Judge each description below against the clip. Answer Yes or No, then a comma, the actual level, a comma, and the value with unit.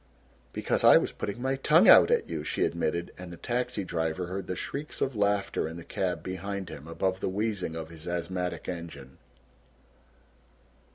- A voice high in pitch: No, very low, 90 Hz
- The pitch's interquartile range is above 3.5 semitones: No, average, 3.2 semitones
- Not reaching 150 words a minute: No, average, 175 wpm